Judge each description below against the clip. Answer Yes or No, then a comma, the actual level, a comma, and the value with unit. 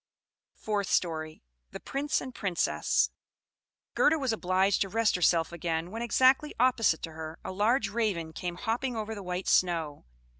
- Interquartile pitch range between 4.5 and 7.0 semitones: Yes, average, 5.2 semitones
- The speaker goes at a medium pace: Yes, average, 155 wpm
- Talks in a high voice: Yes, high, 195 Hz